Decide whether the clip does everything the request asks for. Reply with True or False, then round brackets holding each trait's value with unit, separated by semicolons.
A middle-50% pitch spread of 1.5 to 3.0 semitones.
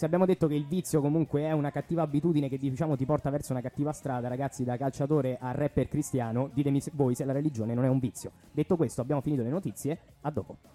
True (2.7 semitones)